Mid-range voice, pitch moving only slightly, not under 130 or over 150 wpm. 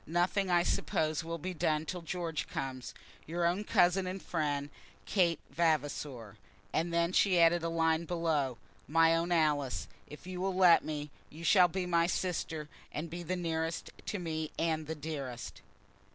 No: medium, 165 Hz; narrow, 2.3 semitones; average, 165 wpm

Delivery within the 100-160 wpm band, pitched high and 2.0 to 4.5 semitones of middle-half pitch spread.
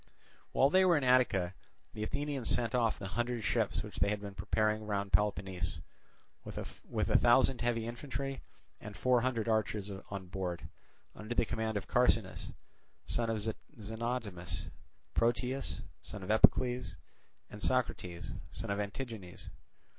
No: average, 140 wpm; low, 110 Hz; average, 3.5 semitones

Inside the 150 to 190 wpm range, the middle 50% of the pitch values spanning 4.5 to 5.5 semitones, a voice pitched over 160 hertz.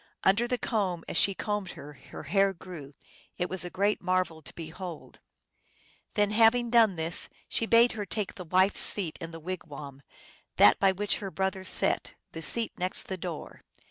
No: average, 180 wpm; average, 3.8 semitones; medium, 185 Hz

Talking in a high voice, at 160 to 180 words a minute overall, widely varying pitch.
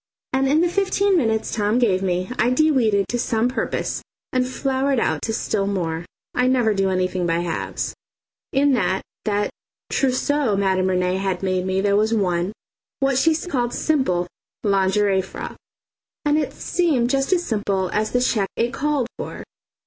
Yes: high, 220 Hz; average, 170 wpm; wide, 5.9 semitones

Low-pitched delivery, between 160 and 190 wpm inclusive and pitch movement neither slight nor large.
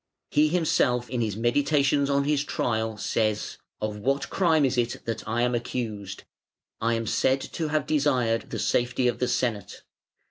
Yes: low, 125 Hz; average, 170 wpm; average, 3.8 semitones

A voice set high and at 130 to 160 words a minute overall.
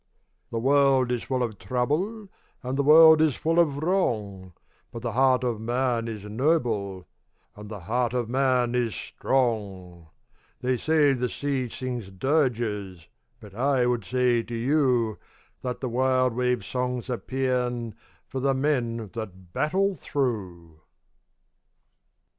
No: low, 125 Hz; average, 140 wpm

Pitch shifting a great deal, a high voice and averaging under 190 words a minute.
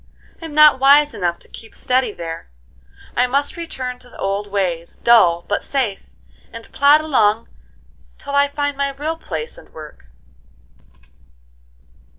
Yes: wide, 6.0 semitones; very high, 255 Hz; average, 145 wpm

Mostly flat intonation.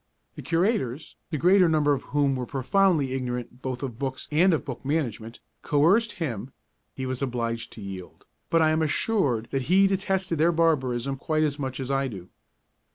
No: average, 4.6 semitones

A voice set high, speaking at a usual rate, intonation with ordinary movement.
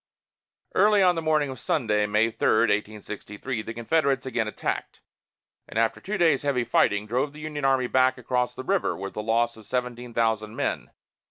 No: low, 125 Hz; average, 180 wpm; average, 4.3 semitones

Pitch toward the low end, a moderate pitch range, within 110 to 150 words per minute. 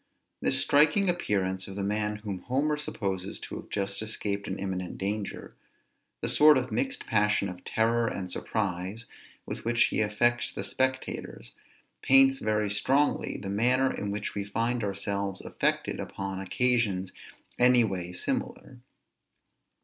Yes: low, 105 Hz; average, 4.1 semitones; average, 140 wpm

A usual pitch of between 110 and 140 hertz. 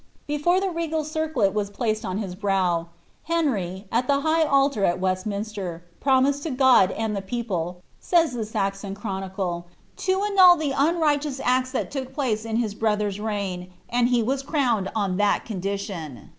No: high, 220 Hz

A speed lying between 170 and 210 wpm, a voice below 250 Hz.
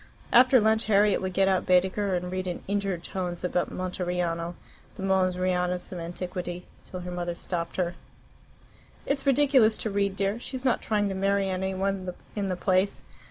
Yes: average, 175 wpm; high, 190 Hz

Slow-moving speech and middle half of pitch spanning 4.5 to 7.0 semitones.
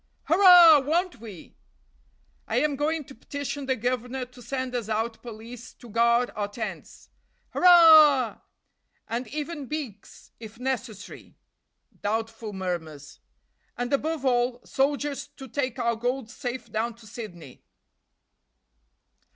No: slow, 120 wpm; average, 4.1 semitones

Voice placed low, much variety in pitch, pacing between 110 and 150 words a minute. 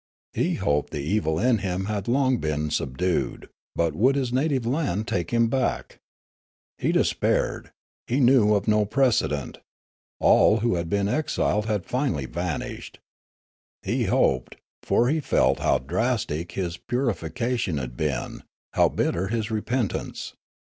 Yes: low, 105 Hz; wide, 6.4 semitones; average, 140 wpm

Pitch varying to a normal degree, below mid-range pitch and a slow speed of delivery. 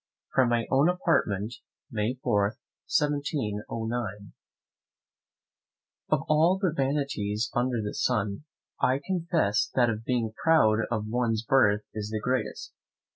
Yes: average, 4.7 semitones; low, 120 Hz; slow, 120 wpm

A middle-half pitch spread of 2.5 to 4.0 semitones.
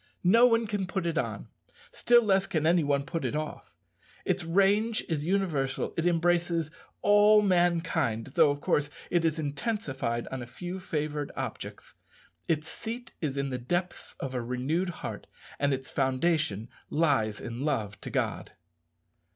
No: average, 5.1 semitones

